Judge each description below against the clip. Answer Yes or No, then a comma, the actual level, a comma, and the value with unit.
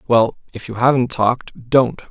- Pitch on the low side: Yes, low, 120 Hz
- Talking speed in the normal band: Yes, average, 170 wpm